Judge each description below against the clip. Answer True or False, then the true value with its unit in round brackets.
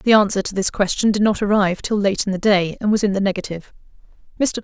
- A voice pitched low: False (200 Hz)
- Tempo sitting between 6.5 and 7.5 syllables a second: True (6.7 syllables/s)